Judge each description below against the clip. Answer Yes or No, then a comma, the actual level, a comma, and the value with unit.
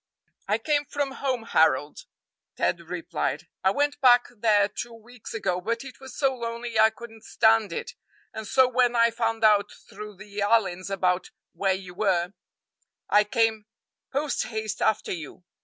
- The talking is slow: No, average, 155 wpm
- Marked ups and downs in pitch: No, average, 3.7 semitones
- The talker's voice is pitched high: Yes, high, 220 Hz